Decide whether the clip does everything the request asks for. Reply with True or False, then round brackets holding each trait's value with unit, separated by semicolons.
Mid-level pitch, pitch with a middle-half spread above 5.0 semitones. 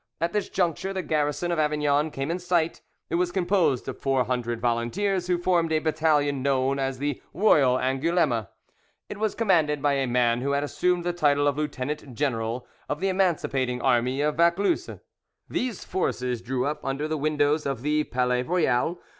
False (145 Hz; 4.7 semitones)